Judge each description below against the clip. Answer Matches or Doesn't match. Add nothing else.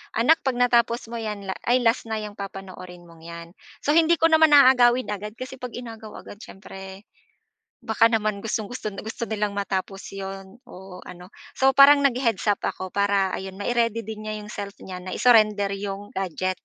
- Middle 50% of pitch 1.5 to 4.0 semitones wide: Matches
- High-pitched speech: Matches